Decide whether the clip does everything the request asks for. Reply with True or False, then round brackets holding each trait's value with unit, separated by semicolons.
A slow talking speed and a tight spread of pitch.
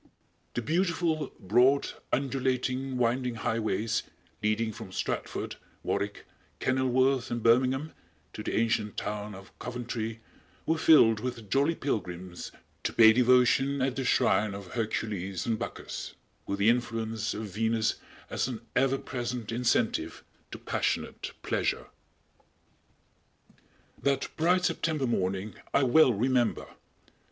False (120 wpm; 3.3 semitones)